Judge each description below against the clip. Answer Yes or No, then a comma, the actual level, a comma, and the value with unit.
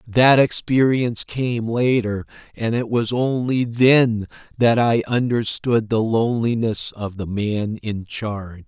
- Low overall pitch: Yes, low, 115 Hz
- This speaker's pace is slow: Yes, slow, 130 wpm